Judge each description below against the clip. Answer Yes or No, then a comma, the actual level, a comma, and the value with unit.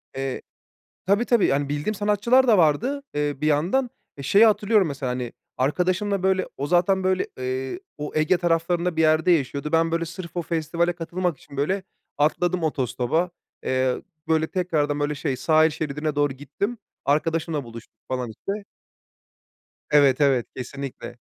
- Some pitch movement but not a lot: Yes, average, 4.5 semitones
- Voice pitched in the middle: Yes, medium, 160 Hz